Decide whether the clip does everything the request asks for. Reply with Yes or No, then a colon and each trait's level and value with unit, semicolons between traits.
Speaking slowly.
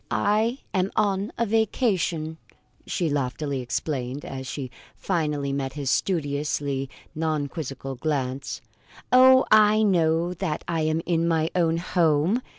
Yes: slow, 130 wpm